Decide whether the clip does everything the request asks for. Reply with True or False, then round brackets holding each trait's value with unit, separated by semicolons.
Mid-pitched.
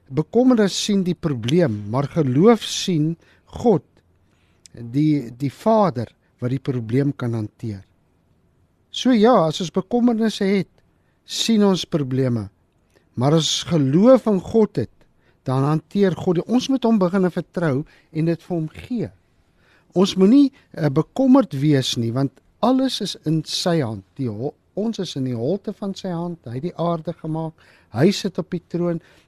True (160 Hz)